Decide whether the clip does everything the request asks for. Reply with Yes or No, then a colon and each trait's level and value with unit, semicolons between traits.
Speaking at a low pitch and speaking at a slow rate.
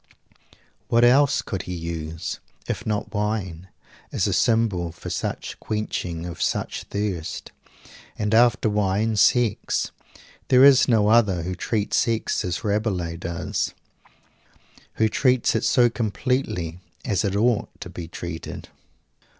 Yes: low, 105 Hz; slow, 130 wpm